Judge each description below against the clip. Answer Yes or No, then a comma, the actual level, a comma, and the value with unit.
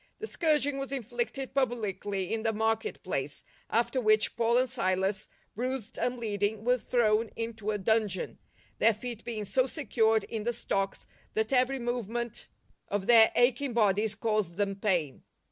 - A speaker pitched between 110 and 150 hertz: No, high, 225 Hz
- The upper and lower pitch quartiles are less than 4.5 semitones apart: Yes, average, 2.9 semitones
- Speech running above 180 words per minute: No, average, 155 wpm